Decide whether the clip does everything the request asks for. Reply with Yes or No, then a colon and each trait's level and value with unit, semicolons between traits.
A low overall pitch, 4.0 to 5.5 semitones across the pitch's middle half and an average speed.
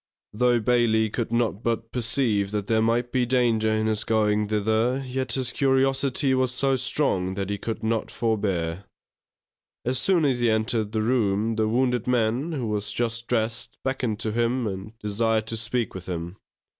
No: low, 115 Hz; narrow, 2.5 semitones; average, 180 wpm